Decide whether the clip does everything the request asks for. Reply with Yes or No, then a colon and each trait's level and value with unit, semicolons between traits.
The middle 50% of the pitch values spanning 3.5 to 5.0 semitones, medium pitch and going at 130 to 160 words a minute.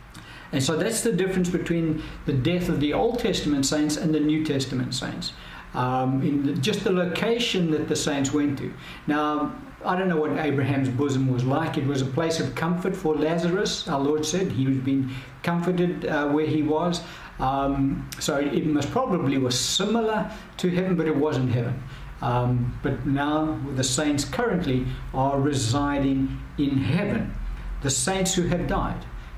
No: average, 4.1 semitones; medium, 150 Hz; average, 175 wpm